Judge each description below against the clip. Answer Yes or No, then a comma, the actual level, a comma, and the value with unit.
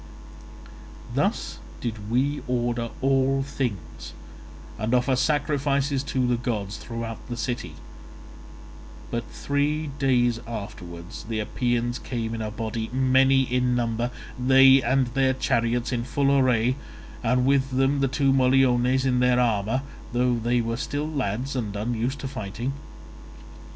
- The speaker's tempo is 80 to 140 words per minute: Yes, slow, 135 wpm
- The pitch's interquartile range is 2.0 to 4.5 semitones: Yes, narrow, 2.4 semitones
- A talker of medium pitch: No, low, 125 Hz